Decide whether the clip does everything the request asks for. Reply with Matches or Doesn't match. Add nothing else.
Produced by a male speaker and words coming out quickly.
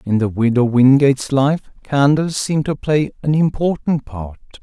Doesn't match